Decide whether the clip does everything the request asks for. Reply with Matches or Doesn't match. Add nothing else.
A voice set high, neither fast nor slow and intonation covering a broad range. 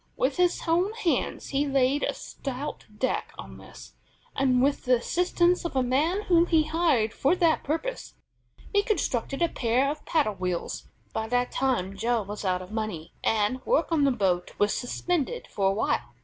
Matches